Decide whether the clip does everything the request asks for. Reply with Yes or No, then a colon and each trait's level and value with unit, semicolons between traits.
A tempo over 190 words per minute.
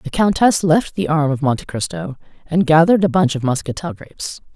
Yes: average, 200 wpm